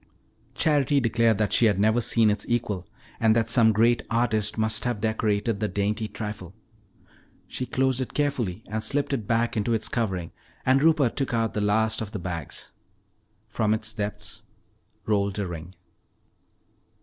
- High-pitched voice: No, low, 110 Hz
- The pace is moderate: Yes, average, 160 wpm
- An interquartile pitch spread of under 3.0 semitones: Yes, narrow, 2.4 semitones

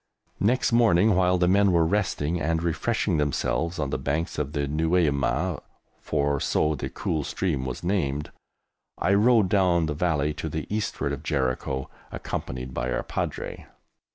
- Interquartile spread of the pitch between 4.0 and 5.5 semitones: Yes, average, 4.4 semitones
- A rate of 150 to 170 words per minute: Yes, average, 155 wpm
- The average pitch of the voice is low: Yes, very low, 80 Hz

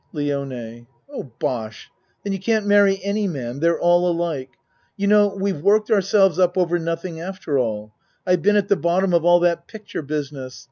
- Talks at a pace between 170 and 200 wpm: Yes, average, 180 wpm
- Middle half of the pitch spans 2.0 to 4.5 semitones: No, wide, 5.4 semitones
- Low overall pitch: No, medium, 175 Hz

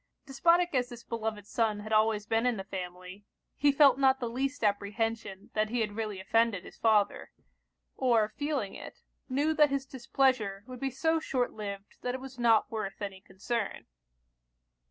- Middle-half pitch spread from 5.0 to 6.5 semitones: No, average, 4.2 semitones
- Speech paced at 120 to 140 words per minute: No, average, 175 wpm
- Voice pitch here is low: No, high, 225 Hz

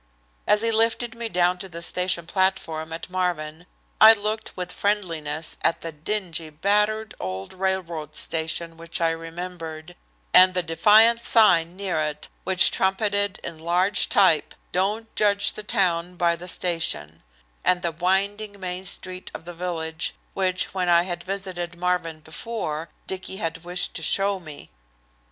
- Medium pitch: Yes, medium, 180 Hz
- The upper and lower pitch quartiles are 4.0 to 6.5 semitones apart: No, average, 3.0 semitones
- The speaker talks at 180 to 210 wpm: No, average, 150 wpm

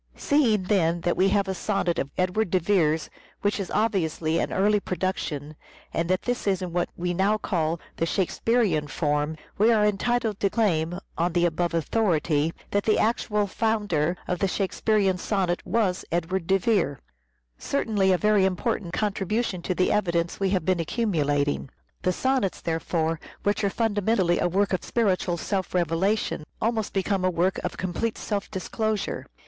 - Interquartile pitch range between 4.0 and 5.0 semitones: No, average, 3.5 semitones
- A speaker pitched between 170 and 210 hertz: Yes, high, 190 Hz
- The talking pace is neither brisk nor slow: Yes, average, 170 wpm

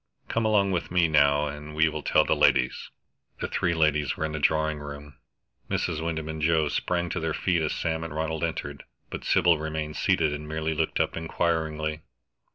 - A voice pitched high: No, very low, 80 Hz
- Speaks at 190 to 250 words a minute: Yes, average, 195 wpm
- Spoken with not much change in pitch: Yes, narrow, 1.4 semitones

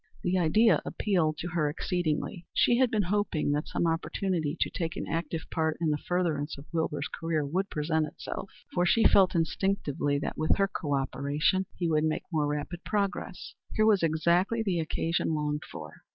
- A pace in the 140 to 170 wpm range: No, average, 180 wpm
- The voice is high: No, medium, 165 Hz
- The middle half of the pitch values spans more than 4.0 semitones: No, average, 3.6 semitones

